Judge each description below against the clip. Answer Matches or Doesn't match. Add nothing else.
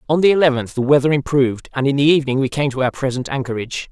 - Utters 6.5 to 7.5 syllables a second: Matches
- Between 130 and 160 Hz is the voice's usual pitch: Matches